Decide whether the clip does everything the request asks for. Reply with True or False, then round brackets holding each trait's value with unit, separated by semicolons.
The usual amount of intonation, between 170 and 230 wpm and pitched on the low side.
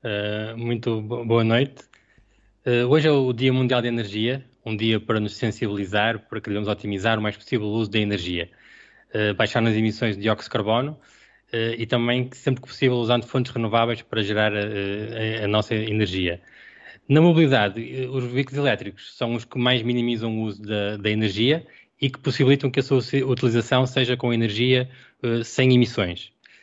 True (3.0 semitones; 180 wpm; 115 Hz)